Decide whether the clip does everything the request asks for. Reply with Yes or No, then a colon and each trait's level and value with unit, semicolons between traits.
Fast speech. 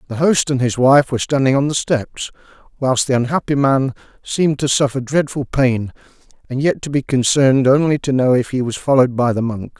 Yes: fast, 210 wpm